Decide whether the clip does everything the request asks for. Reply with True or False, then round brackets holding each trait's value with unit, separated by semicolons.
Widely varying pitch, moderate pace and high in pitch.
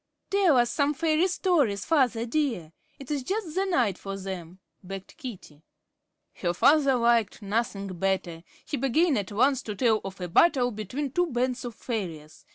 True (6.8 semitones; 165 wpm; 240 Hz)